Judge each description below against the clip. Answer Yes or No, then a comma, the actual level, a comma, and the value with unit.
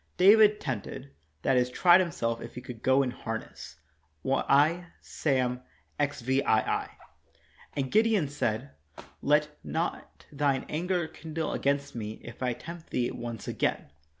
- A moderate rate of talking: No, slow, 130 wpm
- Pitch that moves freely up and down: No, average, 4.7 semitones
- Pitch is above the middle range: No, medium, 140 Hz